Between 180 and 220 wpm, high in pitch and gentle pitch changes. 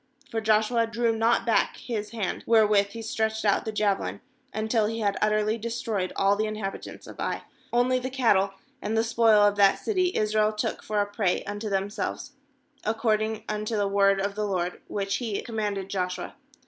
Yes: average, 185 wpm; high, 215 Hz; narrow, 1.9 semitones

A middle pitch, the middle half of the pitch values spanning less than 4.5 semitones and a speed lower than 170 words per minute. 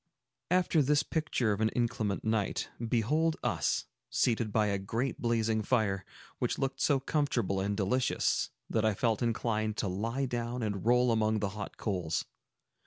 No: low, 115 Hz; average, 3.2 semitones; average, 160 wpm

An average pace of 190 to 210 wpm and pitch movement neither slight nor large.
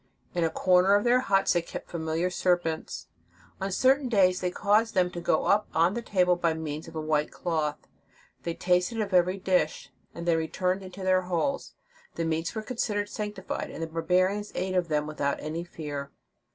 Yes: average, 200 wpm; average, 3.1 semitones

